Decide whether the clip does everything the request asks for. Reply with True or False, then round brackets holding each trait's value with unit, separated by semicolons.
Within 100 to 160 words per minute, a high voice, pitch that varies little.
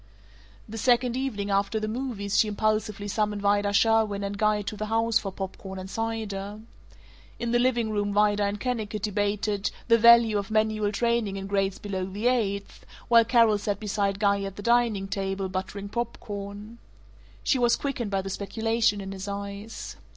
False (180 wpm; 210 Hz; 2.1 semitones)